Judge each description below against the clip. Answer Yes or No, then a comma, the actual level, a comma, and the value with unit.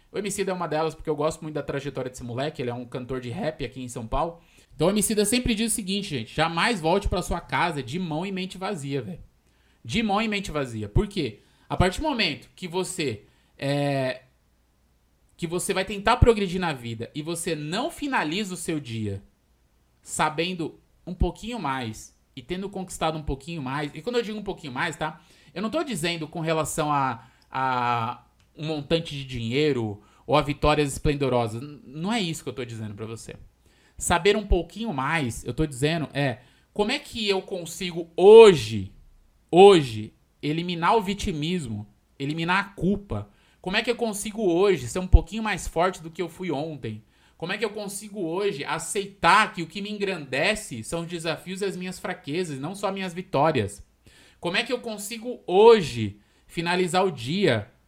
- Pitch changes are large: Yes, wide, 6.6 semitones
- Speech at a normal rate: No, fast, 190 wpm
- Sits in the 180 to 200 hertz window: No, medium, 165 Hz